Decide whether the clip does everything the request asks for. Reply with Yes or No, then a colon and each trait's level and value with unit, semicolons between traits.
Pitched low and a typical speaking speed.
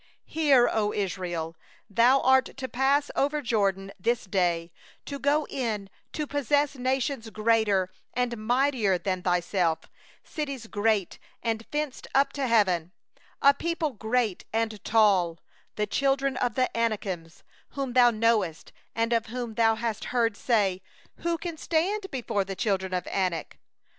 No: high, 230 Hz; average, 145 wpm